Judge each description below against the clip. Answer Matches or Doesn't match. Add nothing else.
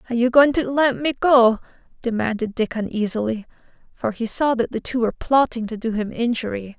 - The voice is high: Matches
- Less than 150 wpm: Doesn't match